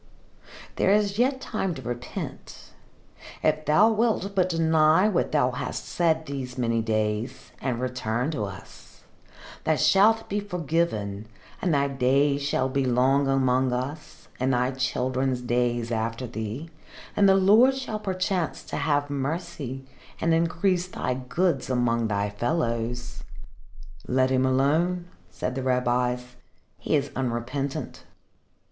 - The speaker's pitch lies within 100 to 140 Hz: Yes, low, 135 Hz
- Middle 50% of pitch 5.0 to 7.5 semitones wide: Yes, average, 5.3 semitones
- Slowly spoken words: Yes, slow, 130 wpm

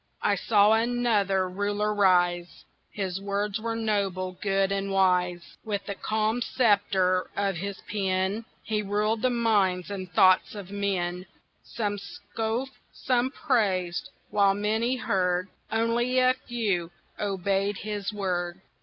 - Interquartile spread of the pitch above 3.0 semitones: No, average, 2.7 semitones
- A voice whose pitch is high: Yes, high, 200 Hz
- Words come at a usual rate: No, slow, 125 wpm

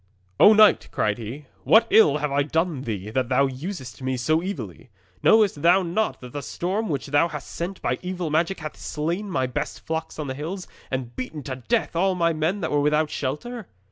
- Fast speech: Yes, fast, 210 wpm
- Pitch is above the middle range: No, medium, 150 Hz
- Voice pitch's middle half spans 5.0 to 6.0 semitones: Yes, wide, 5.5 semitones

